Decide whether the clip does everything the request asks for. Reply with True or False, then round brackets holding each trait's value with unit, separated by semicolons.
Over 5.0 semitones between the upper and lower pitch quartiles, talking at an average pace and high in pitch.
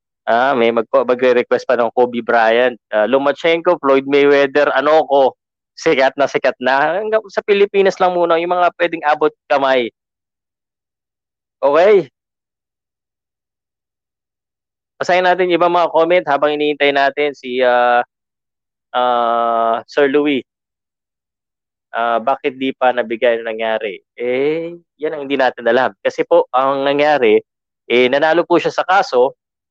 False (5.6 semitones; 130 wpm; 140 Hz)